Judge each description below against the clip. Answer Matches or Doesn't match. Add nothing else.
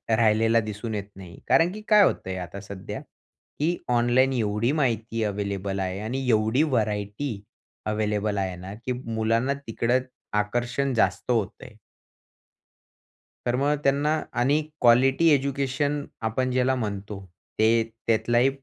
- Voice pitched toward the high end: Doesn't match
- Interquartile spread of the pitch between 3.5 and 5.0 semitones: Matches